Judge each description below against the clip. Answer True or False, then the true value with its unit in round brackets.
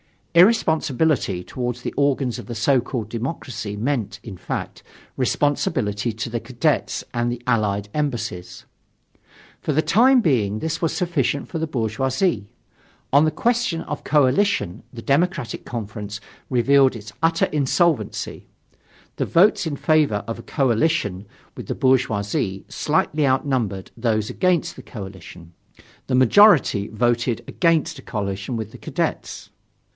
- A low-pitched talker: True (125 Hz)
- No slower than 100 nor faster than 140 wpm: True (135 wpm)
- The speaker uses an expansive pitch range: True (5.9 semitones)